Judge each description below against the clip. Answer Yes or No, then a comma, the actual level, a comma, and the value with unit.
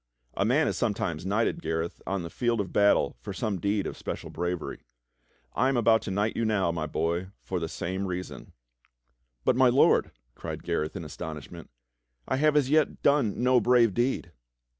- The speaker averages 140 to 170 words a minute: No, average, 180 wpm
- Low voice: Yes, low, 100 Hz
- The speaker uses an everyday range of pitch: No, wide, 5.7 semitones